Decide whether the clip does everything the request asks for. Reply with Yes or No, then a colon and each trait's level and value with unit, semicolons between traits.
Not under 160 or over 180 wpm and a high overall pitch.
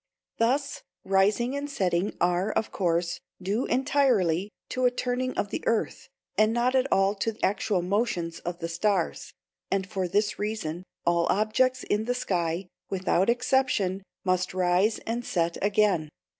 No: average, 150 wpm; high, 200 Hz